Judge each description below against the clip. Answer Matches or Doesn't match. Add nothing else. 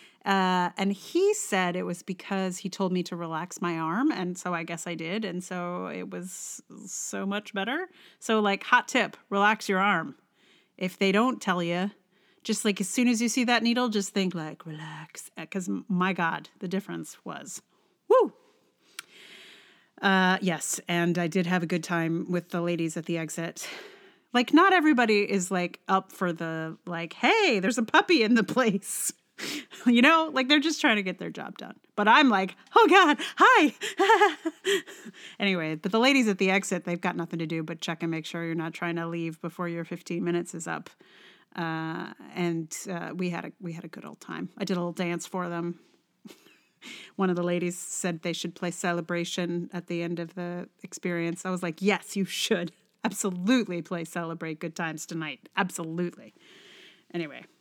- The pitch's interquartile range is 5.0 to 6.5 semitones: Doesn't match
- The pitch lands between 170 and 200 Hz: Matches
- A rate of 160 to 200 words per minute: Matches